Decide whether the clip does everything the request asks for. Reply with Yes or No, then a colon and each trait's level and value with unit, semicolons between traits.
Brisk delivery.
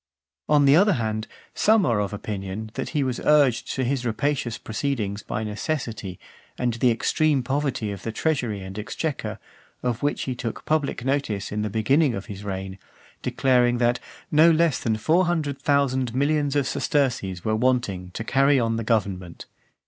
No: average, 170 wpm